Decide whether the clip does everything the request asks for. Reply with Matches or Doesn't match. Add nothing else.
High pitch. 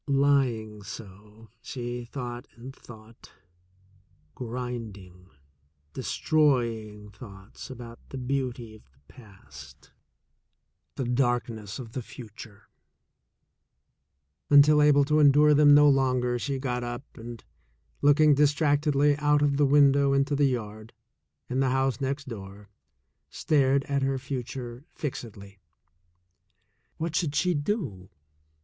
Doesn't match